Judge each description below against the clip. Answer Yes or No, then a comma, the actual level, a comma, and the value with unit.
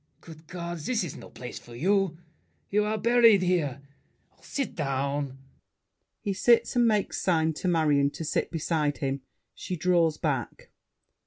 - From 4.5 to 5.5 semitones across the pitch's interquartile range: Yes, average, 5.2 semitones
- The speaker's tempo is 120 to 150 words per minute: Yes, average, 145 wpm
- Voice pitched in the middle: Yes, medium, 165 Hz